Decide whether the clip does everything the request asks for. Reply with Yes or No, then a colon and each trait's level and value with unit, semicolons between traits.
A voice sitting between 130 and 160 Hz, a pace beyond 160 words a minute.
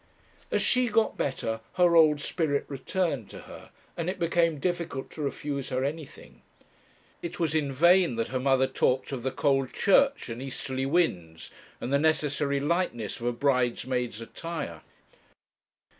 No: medium, 140 Hz; average, 155 wpm